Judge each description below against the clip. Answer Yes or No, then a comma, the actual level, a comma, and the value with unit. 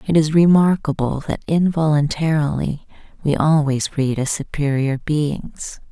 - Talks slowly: Yes, slow, 110 wpm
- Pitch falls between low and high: Yes, medium, 150 Hz